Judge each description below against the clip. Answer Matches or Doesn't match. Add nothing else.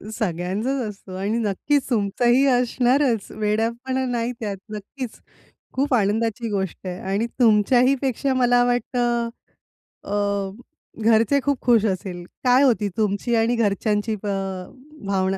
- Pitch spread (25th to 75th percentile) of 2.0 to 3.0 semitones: Doesn't match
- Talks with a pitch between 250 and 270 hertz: Doesn't match